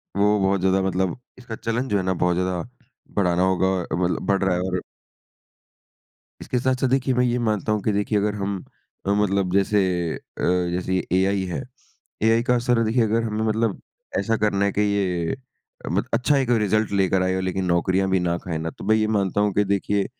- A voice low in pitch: Yes, low, 100 Hz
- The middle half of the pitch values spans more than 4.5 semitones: No, average, 2.8 semitones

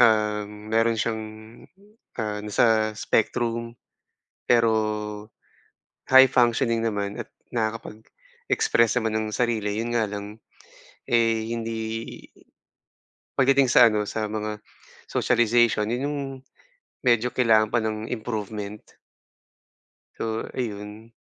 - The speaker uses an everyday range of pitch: No, narrow, 1.7 semitones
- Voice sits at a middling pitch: No, low, 110 Hz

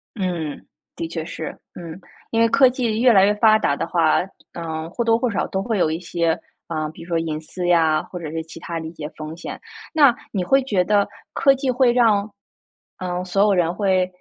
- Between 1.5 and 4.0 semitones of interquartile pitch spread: No, average, 5.3 semitones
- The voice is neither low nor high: Yes, medium, 180 Hz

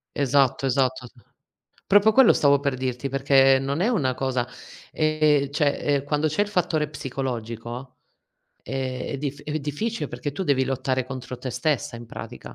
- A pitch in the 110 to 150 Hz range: Yes, low, 135 Hz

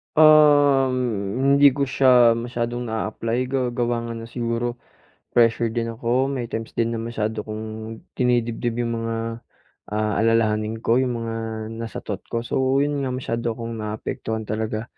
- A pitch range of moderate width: No, narrow, 1.6 semitones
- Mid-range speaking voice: No, low, 115 Hz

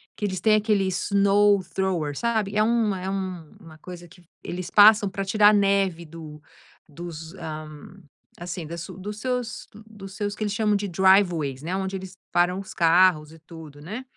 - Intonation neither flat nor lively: Yes, average, 3.4 semitones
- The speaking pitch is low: No, high, 190 Hz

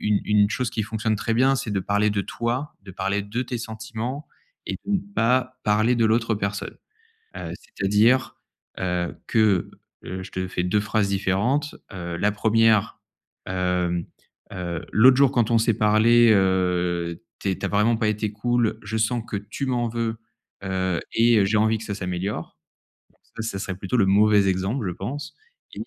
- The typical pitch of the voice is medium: No, low, 105 Hz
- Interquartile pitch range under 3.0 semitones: No, average, 3.3 semitones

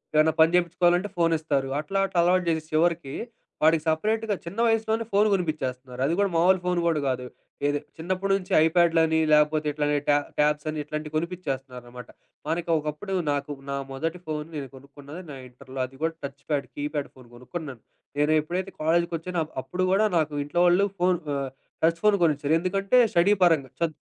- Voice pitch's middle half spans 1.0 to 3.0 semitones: No, average, 3.4 semitones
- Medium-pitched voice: Yes, medium, 160 Hz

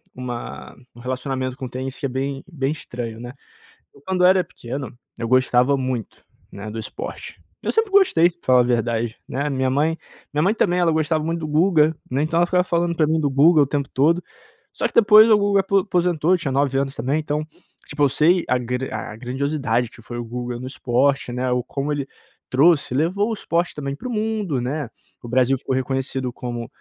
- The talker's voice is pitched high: No, medium, 140 Hz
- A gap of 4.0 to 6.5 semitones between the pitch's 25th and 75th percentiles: Yes, average, 4.8 semitones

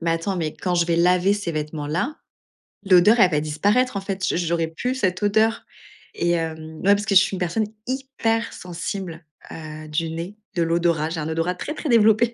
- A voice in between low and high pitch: Yes, medium, 180 Hz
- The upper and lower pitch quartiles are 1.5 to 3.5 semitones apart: No, average, 4.0 semitones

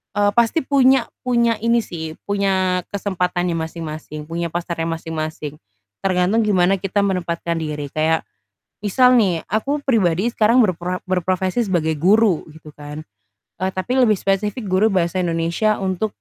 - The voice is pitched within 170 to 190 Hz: Yes, medium, 185 Hz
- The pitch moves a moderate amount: Yes, average, 4.3 semitones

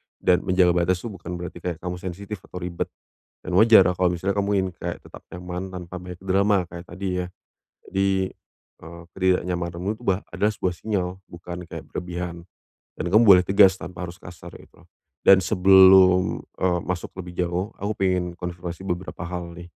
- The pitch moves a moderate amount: No, narrow, 1.4 semitones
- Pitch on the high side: No, very low, 90 Hz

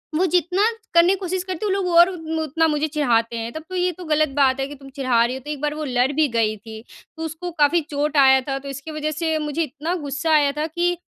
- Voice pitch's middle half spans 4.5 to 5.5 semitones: No, average, 3.4 semitones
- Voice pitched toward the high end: Yes, very high, 300 Hz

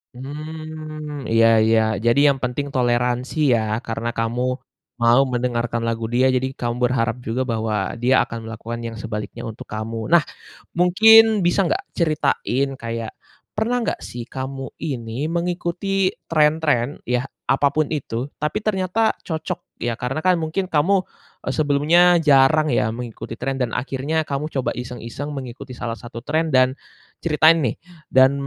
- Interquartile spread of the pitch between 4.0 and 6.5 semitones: Yes, average, 4.9 semitones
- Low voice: Yes, low, 130 Hz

